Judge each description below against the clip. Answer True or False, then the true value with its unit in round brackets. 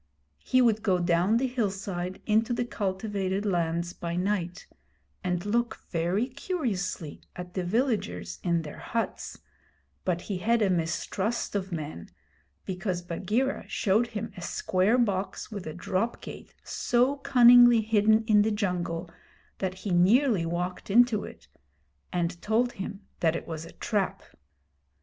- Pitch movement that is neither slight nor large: True (4.2 semitones)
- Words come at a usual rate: True (145 wpm)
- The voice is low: False (195 Hz)